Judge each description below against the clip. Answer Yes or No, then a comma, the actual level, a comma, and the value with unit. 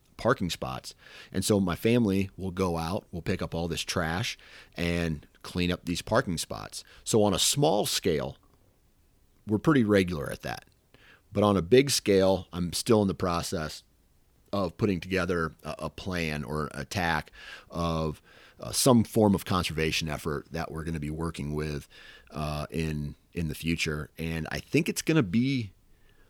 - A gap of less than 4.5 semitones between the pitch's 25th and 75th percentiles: Yes, average, 3.8 semitones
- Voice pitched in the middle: No, very low, 85 Hz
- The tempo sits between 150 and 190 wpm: Yes, average, 170 wpm